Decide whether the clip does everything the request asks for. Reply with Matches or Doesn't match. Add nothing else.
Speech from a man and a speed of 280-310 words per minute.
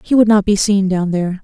Doesn't match